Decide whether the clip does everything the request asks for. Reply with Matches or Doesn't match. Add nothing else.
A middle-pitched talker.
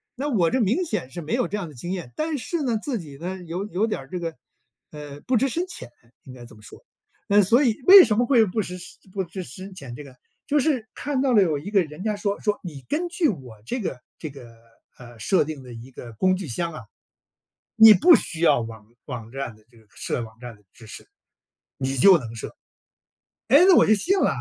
Matches